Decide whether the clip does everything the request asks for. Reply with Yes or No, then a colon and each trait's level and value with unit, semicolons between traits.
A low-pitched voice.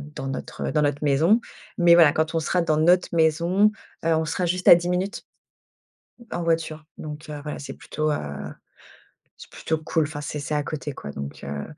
No: medium, 155 Hz